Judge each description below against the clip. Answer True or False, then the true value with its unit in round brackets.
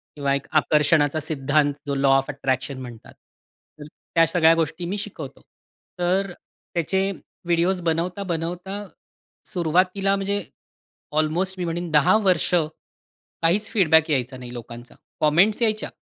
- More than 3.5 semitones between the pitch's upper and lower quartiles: True (4.3 semitones)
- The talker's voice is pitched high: False (165 Hz)